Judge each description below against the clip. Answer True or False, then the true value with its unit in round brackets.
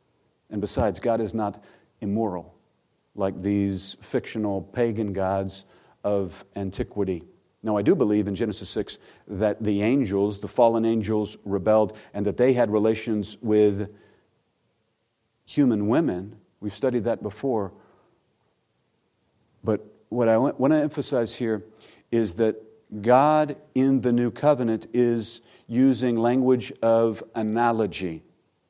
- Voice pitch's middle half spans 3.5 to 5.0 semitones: False (2.4 semitones)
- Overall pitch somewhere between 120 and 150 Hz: False (110 Hz)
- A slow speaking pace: True (120 wpm)